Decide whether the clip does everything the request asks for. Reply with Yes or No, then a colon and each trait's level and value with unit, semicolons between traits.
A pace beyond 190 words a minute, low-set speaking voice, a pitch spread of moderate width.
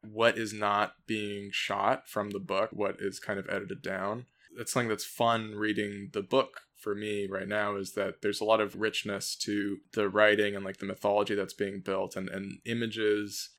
No: average, 200 wpm; low, 105 Hz; narrow, 1.3 semitones